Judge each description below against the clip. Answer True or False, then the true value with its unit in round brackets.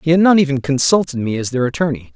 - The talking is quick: True (250 wpm)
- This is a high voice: False (150 Hz)